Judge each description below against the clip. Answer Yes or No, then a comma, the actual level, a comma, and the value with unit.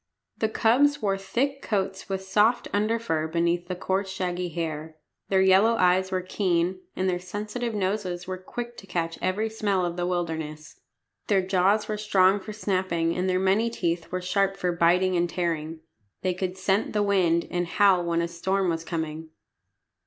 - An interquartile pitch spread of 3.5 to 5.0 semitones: No, average, 2.7 semitones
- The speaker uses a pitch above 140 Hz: Yes, medium, 185 Hz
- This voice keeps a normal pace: Yes, average, 180 wpm